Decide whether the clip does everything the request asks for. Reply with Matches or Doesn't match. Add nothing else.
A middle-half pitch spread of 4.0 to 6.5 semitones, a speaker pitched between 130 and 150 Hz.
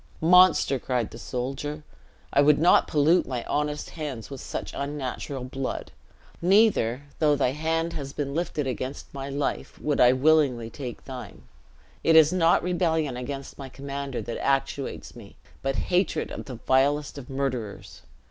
Doesn't match